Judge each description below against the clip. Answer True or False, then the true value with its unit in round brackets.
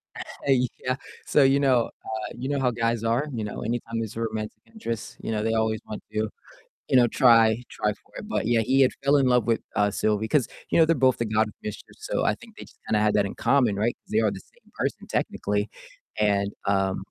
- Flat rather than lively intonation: False (3.1 semitones)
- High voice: False (115 Hz)